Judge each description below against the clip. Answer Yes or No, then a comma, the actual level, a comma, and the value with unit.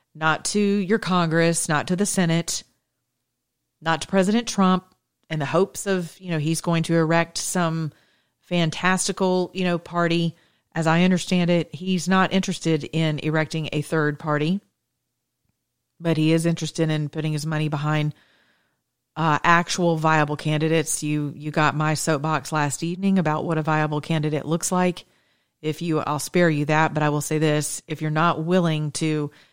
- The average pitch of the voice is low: No, medium, 160 Hz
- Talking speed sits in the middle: Yes, average, 165 wpm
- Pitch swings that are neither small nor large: No, narrow, 2.3 semitones